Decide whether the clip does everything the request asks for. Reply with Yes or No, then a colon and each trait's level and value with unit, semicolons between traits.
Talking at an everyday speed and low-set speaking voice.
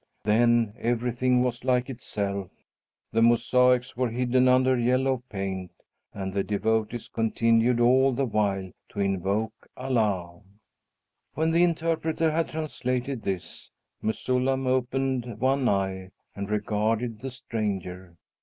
No: slow, 120 wpm; low, 120 Hz